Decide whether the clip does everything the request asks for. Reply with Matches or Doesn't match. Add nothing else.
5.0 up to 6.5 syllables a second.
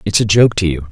Matches